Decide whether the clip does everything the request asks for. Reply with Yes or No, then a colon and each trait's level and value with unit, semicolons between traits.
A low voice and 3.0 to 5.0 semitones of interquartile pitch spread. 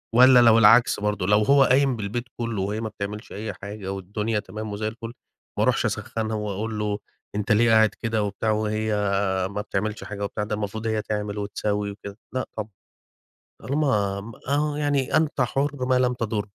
No: low, 110 Hz; narrow, 2.4 semitones